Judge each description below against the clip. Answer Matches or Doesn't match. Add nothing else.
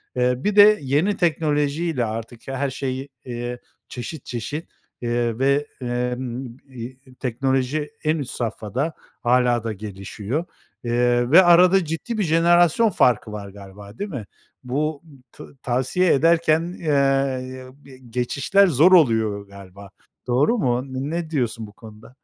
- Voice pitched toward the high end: Doesn't match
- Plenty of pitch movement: Doesn't match